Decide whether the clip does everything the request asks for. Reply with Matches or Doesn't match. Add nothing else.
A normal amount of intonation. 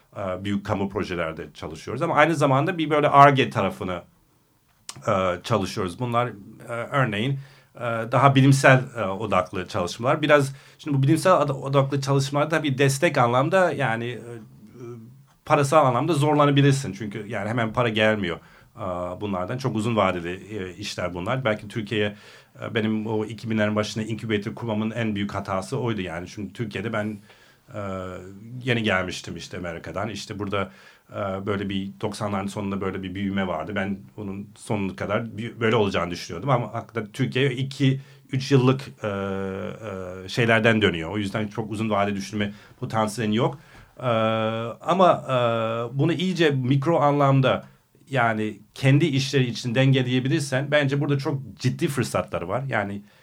Matches